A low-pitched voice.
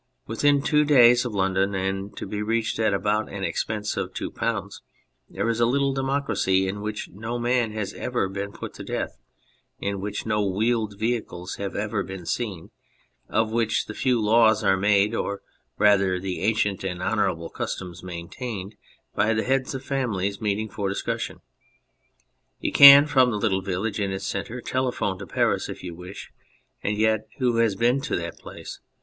Yes: low, 105 Hz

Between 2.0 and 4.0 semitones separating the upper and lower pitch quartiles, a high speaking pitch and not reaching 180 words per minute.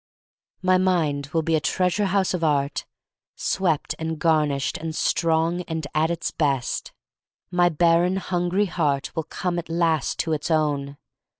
No: narrow, 2.6 semitones; medium, 165 Hz; average, 155 wpm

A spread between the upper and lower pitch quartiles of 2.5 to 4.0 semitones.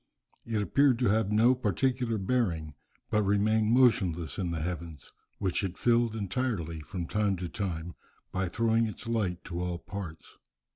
No: average, 4.7 semitones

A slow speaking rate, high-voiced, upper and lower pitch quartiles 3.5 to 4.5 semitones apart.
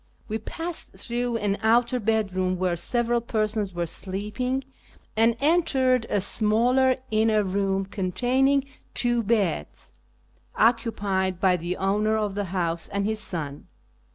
Yes: slow, 125 wpm; high, 215 Hz; average, 4.0 semitones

